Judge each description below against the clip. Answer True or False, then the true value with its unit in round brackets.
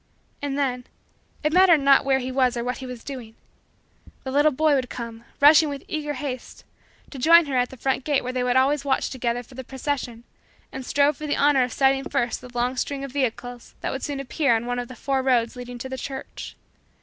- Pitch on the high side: True (265 Hz)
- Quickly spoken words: True (225 wpm)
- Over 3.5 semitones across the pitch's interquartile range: False (2.4 semitones)